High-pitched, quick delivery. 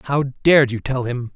No: low, 130 Hz; fast, 220 wpm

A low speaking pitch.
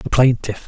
Yes: low, 120 Hz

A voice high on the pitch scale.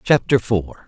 No: low, 110 Hz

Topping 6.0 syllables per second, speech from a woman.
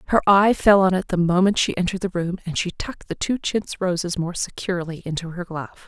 Yes: 6.2 syllables/s; female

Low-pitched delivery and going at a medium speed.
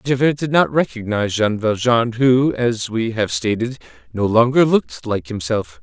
Yes: low, 120 Hz; average, 165 wpm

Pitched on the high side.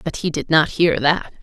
No: medium, 160 Hz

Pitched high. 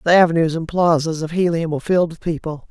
No: medium, 165 Hz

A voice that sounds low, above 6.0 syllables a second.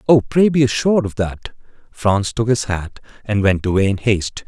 No: low, 110 Hz; 5.2 syllables/s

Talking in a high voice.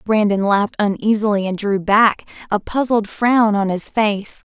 Yes: high, 210 Hz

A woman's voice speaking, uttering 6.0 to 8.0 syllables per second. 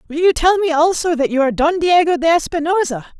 Yes: female; 6.1 syllables/s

